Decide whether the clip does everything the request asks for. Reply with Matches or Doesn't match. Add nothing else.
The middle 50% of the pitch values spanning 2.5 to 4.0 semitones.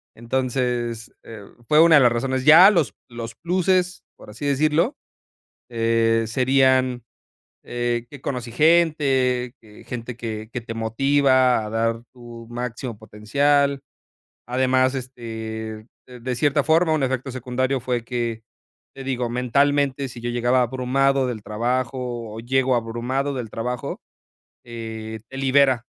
Matches